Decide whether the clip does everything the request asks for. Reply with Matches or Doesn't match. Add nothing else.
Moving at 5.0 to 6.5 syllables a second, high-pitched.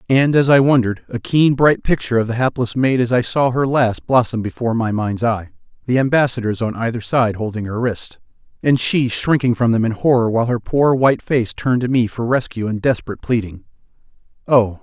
Doesn't match